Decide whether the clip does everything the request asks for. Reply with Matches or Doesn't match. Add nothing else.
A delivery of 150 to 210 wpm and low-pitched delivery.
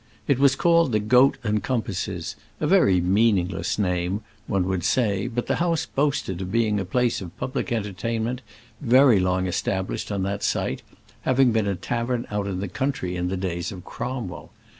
Matches